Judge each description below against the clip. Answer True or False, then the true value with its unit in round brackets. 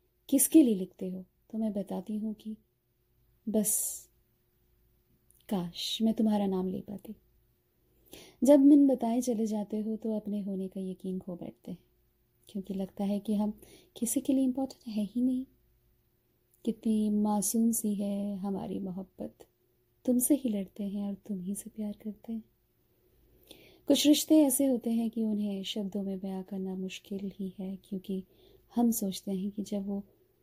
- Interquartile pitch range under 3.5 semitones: True (2.9 semitones)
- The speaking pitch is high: True (205 Hz)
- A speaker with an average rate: True (160 wpm)